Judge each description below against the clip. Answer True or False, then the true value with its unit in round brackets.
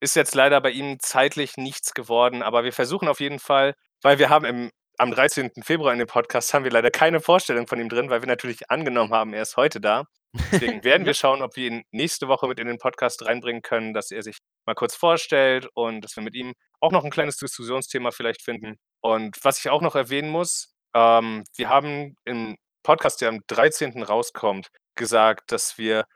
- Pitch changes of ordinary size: True (3.3 semitones)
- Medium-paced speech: False (215 wpm)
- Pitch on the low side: True (125 Hz)